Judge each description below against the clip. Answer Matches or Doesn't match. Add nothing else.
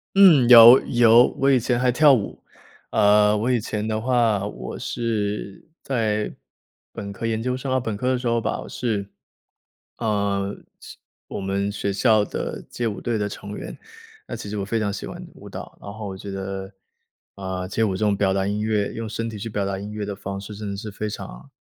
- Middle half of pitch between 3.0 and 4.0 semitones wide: Doesn't match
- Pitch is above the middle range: Doesn't match